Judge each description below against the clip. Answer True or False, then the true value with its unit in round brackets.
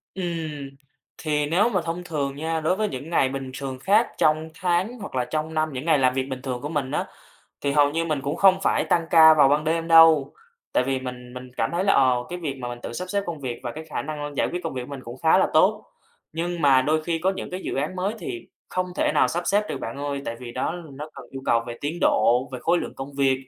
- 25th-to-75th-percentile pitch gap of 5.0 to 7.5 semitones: False (4.2 semitones)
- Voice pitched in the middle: True (150 Hz)